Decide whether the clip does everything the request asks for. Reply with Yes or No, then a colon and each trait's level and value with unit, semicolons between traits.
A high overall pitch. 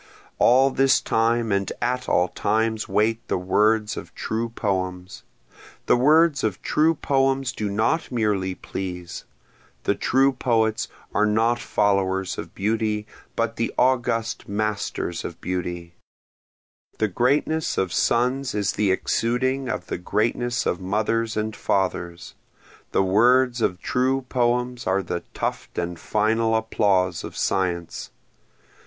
No: low, 110 Hz